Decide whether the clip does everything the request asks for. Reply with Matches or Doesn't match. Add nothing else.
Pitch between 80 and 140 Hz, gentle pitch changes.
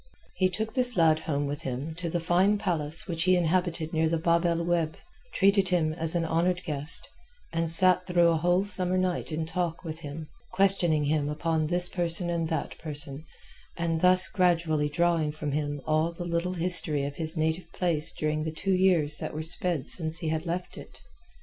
Doesn't match